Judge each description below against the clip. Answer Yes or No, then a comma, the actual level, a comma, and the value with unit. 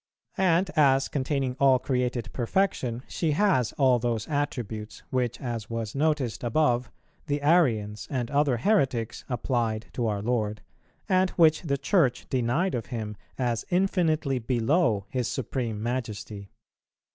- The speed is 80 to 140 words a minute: Yes, slow, 135 wpm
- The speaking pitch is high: No, low, 125 Hz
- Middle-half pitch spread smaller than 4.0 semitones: No, average, 4.3 semitones